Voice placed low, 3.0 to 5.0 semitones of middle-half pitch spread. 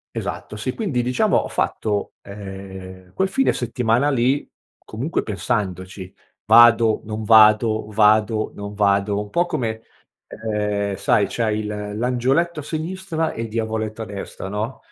Yes: low, 110 Hz; average, 3.3 semitones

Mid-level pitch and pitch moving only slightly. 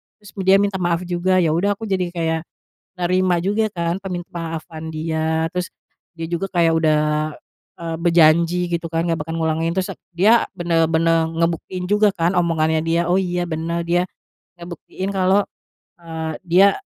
Yes: medium, 170 Hz; narrow, 2.0 semitones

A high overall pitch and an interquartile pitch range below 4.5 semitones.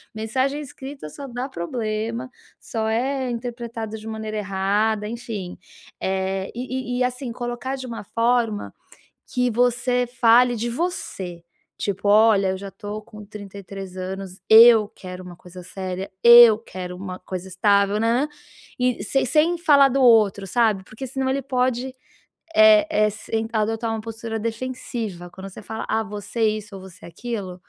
Yes: high, 220 Hz; average, 3.9 semitones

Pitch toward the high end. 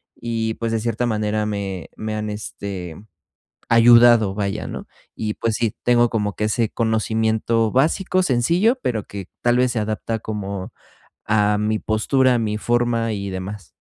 No: low, 110 Hz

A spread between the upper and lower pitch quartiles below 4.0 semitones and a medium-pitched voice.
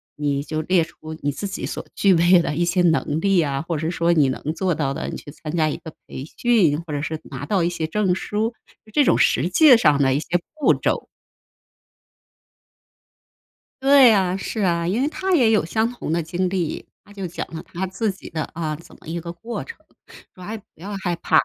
No: average, 4.3 semitones; medium, 175 Hz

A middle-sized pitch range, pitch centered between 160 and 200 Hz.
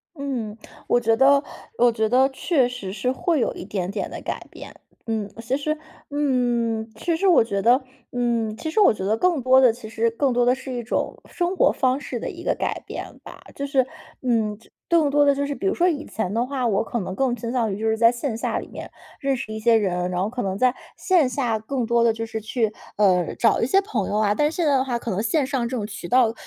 No: average, 3.8 semitones; high, 240 Hz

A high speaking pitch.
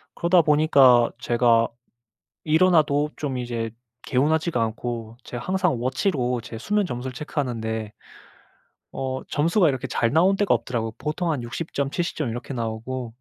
No: low, 130 Hz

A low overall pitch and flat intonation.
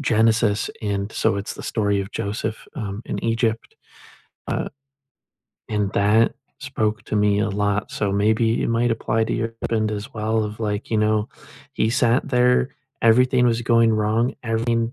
Yes: low, 110 Hz; narrow, 1.7 semitones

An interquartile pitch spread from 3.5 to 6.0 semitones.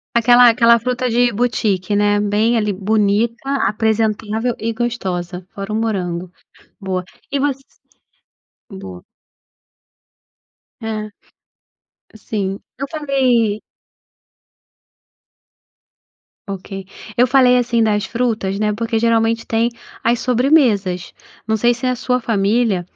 No: average, 2.9 semitones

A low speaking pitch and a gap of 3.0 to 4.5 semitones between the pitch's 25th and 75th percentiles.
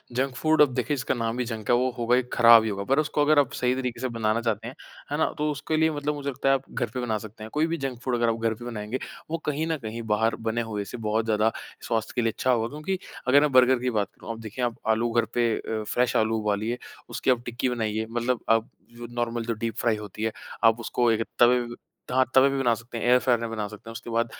No: low, 120 Hz; narrow, 2.4 semitones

